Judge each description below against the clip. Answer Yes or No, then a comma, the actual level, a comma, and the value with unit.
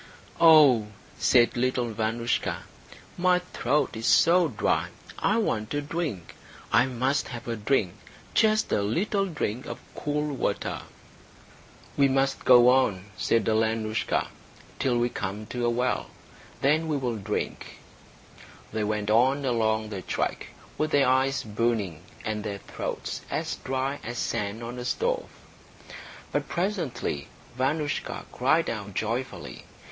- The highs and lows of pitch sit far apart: No, average, 4.7 semitones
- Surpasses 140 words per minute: No, slow, 135 wpm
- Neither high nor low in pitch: No, low, 125 Hz